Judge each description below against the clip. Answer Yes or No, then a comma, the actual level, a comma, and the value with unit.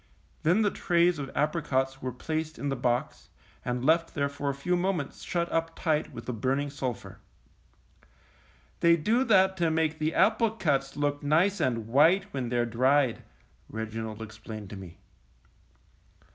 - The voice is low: No, medium, 145 Hz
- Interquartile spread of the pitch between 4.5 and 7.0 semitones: Yes, average, 5.0 semitones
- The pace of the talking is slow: No, average, 150 wpm